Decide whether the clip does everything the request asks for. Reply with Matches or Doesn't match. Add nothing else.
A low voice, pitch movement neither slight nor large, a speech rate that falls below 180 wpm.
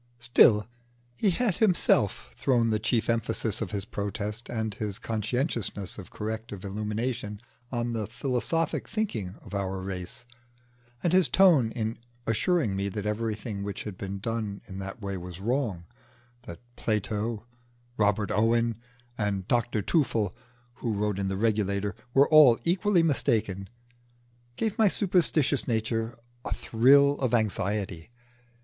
Matches